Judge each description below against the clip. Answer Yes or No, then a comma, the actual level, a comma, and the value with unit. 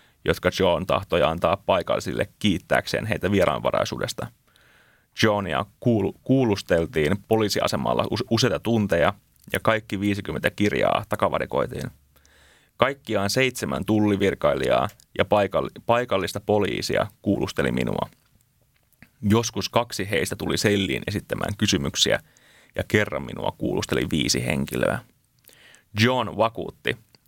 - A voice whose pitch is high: No, low, 105 Hz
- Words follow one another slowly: Yes, slow, 90 wpm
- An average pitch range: Yes, average, 3.7 semitones